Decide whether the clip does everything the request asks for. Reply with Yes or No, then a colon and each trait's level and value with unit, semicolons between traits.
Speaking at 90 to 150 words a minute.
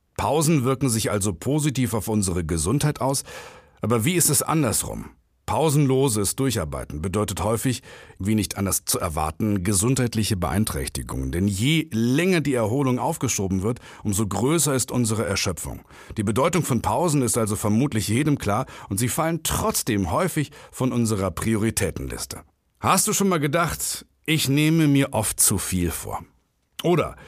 Yes: average, 145 wpm